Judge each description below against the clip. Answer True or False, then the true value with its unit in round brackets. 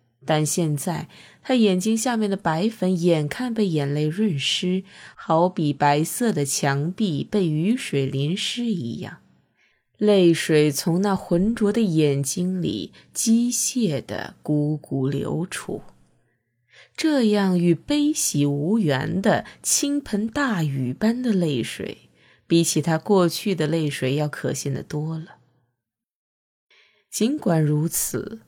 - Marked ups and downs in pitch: True (6.2 semitones)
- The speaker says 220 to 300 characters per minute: False (175 characters per minute)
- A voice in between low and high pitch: True (170 Hz)